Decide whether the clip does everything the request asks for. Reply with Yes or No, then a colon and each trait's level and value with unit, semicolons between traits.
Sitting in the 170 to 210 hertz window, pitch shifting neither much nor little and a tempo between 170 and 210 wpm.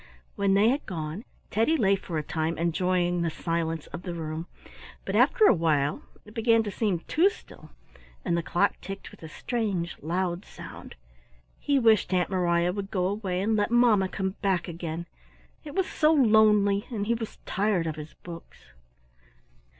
Yes: high, 190 Hz; average, 4.2 semitones; average, 175 wpm